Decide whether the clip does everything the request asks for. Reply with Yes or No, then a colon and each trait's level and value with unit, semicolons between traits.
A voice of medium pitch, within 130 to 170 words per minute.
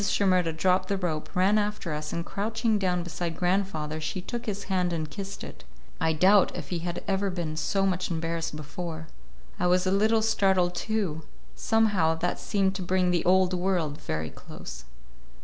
No: medium, 180 Hz; average, 180 wpm